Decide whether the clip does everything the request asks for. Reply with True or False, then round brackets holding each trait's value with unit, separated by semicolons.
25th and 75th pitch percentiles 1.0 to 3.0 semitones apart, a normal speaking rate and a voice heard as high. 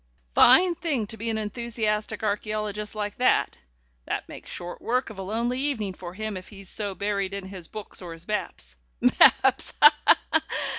True (2.5 semitones; 180 wpm; 210 Hz)